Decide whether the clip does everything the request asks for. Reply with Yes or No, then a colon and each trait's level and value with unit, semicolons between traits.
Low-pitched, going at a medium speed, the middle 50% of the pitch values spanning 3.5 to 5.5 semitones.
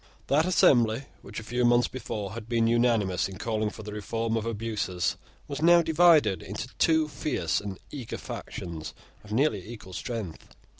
Yes: low, 115 Hz; average, 165 wpm; average, 3.8 semitones